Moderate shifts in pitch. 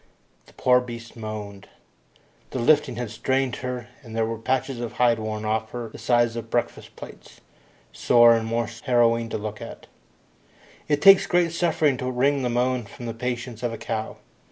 No: narrow, 2.0 semitones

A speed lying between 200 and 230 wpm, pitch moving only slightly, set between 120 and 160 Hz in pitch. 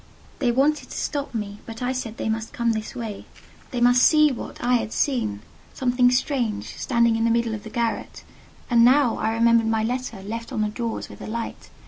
No: fast, 205 wpm; narrow, 2.0 semitones; high, 235 Hz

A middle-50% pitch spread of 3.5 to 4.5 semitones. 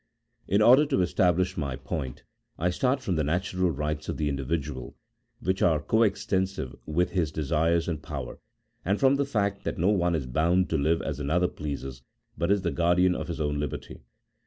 Yes: average, 3.9 semitones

